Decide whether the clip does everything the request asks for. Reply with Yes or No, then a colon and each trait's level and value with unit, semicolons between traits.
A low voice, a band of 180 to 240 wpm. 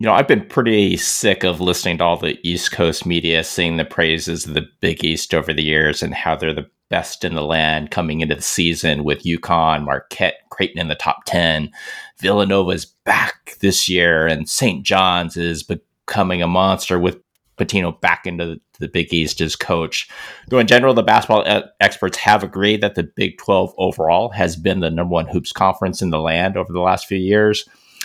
Yes: very low, 85 Hz; average, 200 wpm